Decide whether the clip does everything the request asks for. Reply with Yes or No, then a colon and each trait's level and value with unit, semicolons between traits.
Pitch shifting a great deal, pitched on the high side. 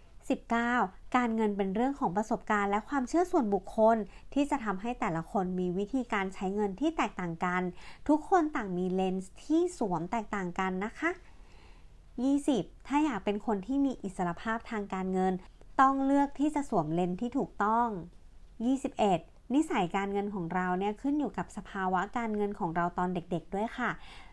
Yes: wide, 5.9 semitones; high, 210 Hz